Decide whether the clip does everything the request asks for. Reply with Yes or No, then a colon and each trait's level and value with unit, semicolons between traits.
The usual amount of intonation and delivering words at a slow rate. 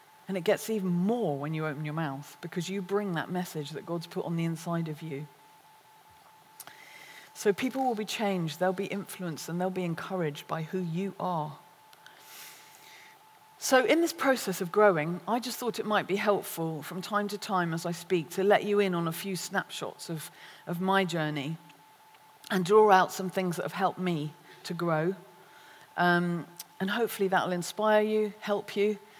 No: average, 3.8 semitones; average, 185 wpm